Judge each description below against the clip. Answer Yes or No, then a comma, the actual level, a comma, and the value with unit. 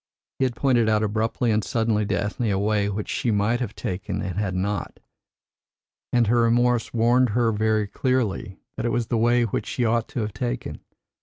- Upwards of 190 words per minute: Yes, average, 200 wpm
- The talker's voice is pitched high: No, low, 115 Hz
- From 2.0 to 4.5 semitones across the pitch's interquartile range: Yes, narrow, 2.6 semitones